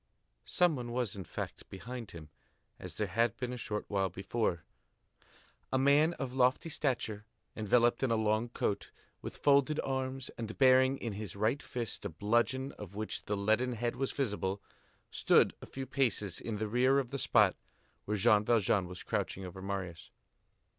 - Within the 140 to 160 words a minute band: No, average, 175 wpm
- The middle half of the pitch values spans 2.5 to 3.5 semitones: No, average, 4.2 semitones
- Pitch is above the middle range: No, low, 115 Hz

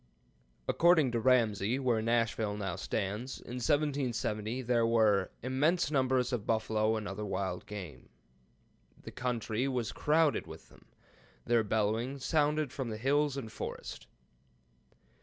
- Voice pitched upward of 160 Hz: No, low, 120 Hz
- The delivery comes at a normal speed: No, slow, 130 wpm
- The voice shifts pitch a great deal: No, average, 3.8 semitones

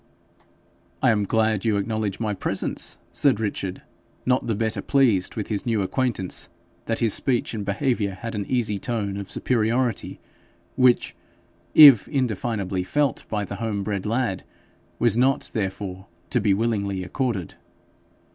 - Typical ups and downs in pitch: Yes, average, 3.2 semitones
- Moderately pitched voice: No, low, 110 Hz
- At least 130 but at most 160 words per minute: Yes, average, 145 wpm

